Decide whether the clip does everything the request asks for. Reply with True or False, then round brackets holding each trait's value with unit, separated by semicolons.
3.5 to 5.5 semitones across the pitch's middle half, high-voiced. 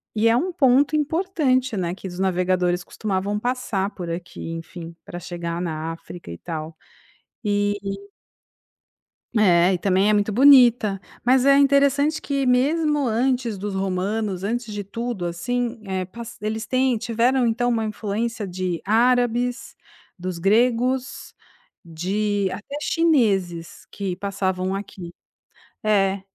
True (5.0 semitones; 210 Hz)